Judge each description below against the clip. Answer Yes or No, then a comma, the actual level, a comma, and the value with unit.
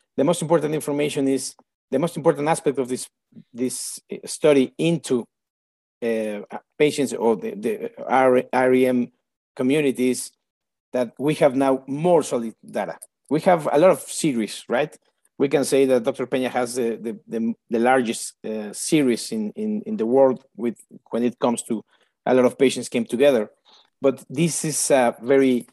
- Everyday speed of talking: Yes, average, 165 wpm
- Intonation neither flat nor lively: Yes, average, 3.5 semitones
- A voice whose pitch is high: No, low, 130 Hz